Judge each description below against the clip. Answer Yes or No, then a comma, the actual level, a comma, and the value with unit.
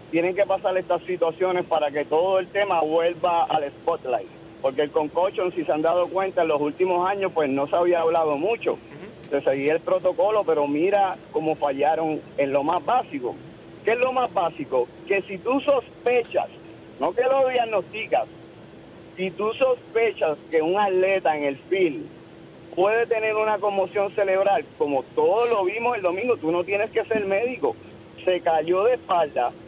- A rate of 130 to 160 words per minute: No, average, 175 wpm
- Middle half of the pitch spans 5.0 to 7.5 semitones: Yes, wide, 5.5 semitones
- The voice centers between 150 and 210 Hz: Yes, high, 190 Hz